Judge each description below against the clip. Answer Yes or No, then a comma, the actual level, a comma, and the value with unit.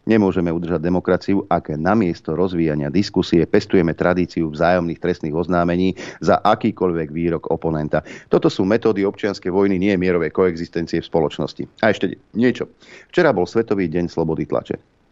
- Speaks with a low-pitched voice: Yes, very low, 90 Hz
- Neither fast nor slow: Yes, average, 145 wpm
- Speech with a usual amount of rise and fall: No, narrow, 2.2 semitones